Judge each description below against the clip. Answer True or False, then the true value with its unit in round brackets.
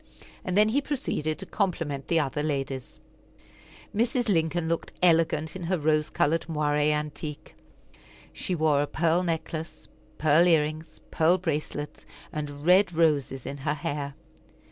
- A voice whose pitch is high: False (155 Hz)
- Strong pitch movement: False (2.8 semitones)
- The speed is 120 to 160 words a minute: True (145 wpm)